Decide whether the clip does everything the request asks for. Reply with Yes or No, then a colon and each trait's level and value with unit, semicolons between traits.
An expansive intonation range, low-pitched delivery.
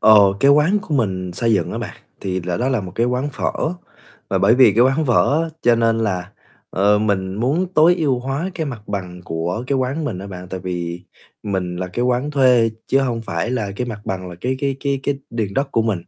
Yes: wide, 6.1 semitones; low, 115 Hz